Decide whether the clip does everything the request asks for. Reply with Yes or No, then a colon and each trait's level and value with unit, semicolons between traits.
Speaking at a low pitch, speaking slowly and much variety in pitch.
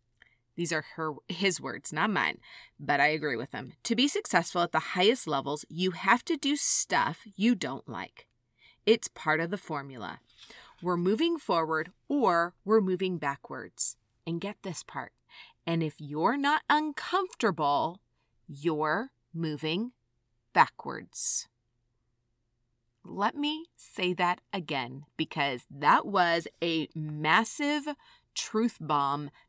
No: medium, 170 Hz; slow, 130 wpm; wide, 7.5 semitones